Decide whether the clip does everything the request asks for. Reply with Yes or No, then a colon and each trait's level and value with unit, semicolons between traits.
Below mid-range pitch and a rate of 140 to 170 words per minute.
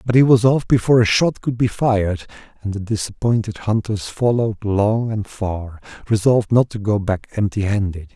No: low, 110 Hz; average, 185 wpm